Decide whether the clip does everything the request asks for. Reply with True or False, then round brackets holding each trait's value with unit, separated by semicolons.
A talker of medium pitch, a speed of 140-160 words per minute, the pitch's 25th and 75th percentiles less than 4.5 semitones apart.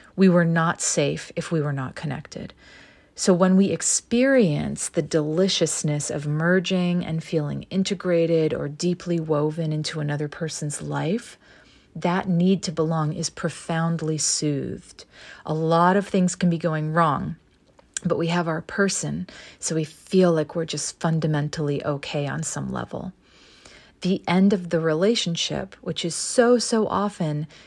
True (165 Hz; 150 wpm; 2.9 semitones)